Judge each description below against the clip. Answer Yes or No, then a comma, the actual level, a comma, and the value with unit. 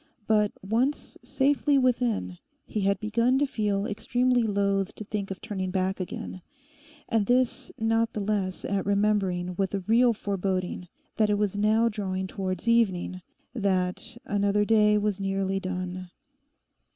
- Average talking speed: Yes, average, 145 wpm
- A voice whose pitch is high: Yes, high, 205 Hz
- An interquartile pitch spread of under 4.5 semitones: Yes, average, 2.8 semitones